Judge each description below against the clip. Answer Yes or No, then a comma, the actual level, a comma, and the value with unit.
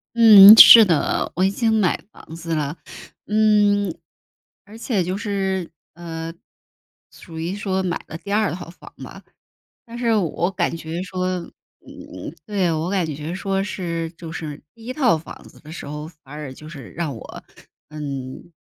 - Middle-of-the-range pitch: Yes, medium, 175 Hz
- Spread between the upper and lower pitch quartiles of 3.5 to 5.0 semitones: Yes, average, 4.0 semitones